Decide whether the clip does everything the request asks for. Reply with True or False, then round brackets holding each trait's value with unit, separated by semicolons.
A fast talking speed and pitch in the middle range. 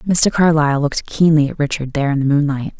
True (215 wpm; 150 Hz)